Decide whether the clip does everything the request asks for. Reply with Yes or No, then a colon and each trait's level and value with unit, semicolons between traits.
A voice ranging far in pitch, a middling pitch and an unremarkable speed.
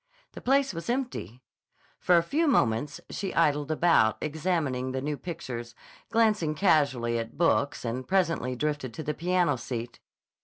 Yes: wide, 5.8 semitones; medium, 150 Hz; average, 150 wpm